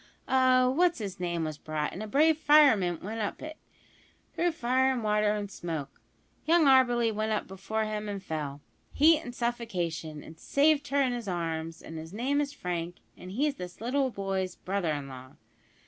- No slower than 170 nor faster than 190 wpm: Yes, average, 180 wpm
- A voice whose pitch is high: Yes, high, 210 Hz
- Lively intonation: Yes, wide, 7.1 semitones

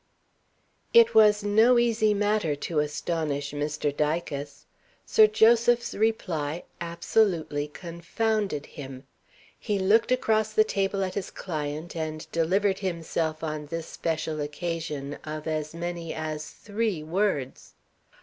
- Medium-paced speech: No, slow, 120 wpm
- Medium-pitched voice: Yes, medium, 170 Hz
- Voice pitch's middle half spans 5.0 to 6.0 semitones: Yes, wide, 5.5 semitones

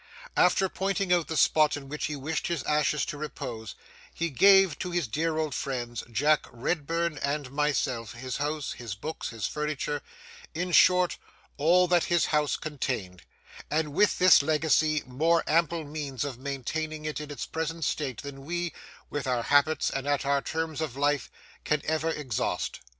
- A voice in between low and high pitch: Yes, medium, 150 Hz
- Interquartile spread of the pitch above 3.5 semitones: No, average, 2.8 semitones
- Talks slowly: No, average, 165 wpm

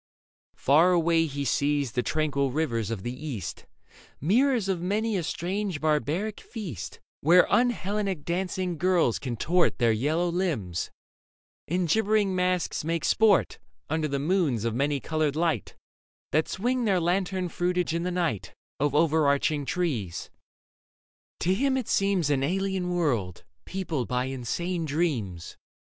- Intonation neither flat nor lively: Yes, average, 4.8 semitones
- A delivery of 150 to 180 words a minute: No, average, 140 wpm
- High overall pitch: No, medium, 165 Hz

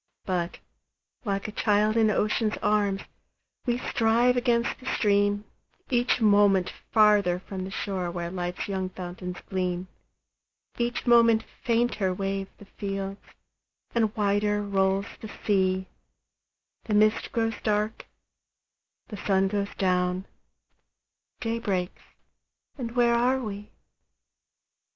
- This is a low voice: No, high, 205 Hz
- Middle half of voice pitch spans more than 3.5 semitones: No, average, 2.8 semitones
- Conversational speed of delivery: No, slow, 115 wpm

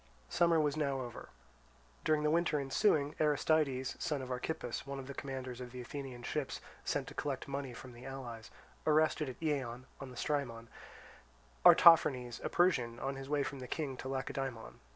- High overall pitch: No, low, 135 Hz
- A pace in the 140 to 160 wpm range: No, average, 175 wpm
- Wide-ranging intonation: No, average, 3.0 semitones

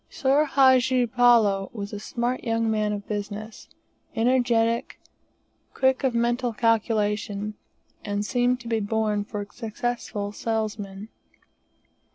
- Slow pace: Yes, slow, 120 wpm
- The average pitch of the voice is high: Yes, high, 225 Hz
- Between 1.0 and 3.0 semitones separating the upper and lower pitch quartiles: Yes, average, 2.7 semitones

